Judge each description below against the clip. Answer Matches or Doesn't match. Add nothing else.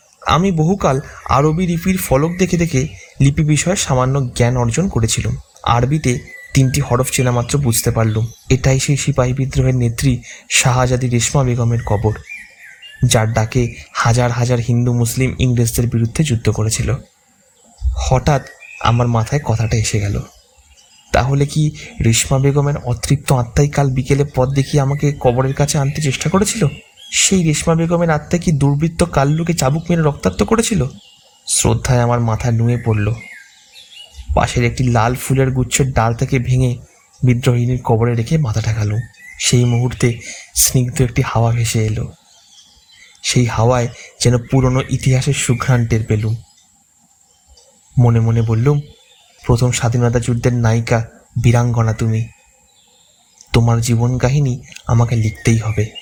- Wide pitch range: Doesn't match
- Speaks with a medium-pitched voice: Doesn't match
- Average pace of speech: Doesn't match